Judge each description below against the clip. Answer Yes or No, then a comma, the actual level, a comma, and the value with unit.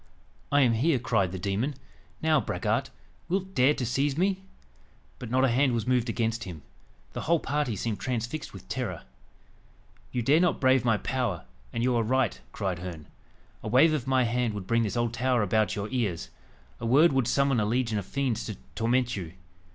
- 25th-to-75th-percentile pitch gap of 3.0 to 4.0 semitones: Yes, average, 3.5 semitones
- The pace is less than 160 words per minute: No, average, 195 wpm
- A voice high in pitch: No, low, 120 Hz